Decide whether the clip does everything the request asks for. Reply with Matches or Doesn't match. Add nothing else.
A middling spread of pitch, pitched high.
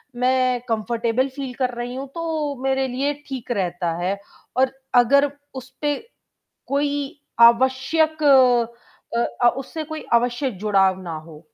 Matches